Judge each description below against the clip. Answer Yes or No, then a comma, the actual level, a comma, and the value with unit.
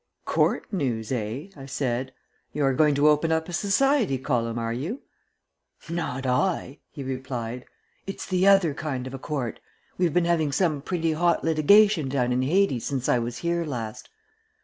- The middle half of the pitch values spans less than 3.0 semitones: No, average, 5.1 semitones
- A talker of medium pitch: Yes, medium, 145 Hz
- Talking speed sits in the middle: Yes, average, 170 wpm